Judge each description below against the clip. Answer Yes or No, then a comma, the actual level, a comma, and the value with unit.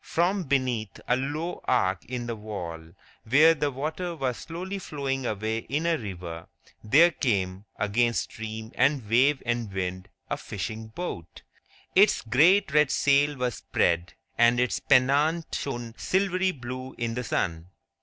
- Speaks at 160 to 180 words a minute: No, average, 145 wpm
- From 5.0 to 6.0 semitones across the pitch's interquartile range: Yes, wide, 5.5 semitones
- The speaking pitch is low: Yes, low, 125 Hz